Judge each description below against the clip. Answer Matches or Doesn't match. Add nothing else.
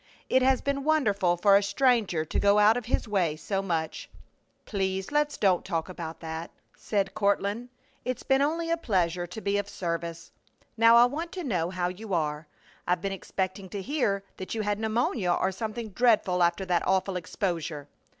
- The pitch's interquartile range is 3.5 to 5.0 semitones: Matches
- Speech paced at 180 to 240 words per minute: Matches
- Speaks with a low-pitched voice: Doesn't match